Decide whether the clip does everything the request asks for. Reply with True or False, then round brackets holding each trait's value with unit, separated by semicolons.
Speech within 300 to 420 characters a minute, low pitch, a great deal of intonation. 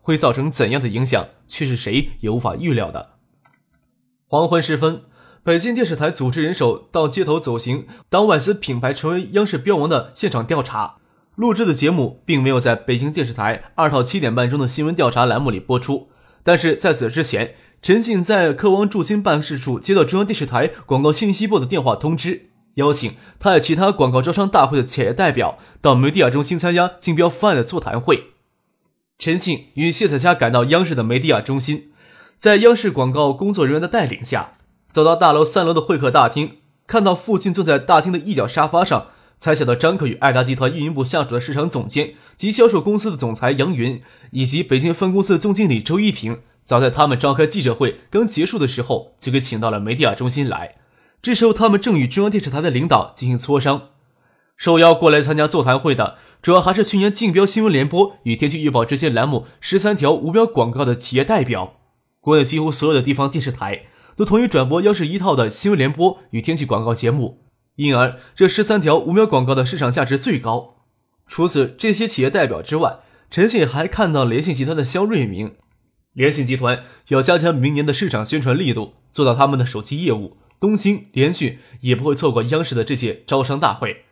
False (320 characters per minute; 150 Hz; 5.7 semitones)